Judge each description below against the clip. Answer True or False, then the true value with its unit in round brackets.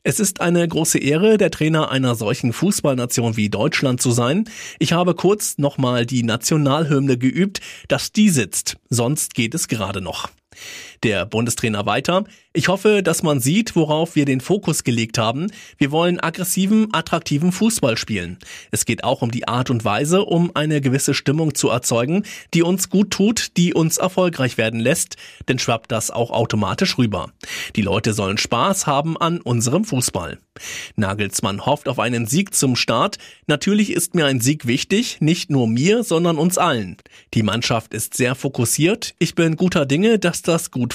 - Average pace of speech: True (170 wpm)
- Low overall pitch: False (145 Hz)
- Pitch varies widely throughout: True (6.7 semitones)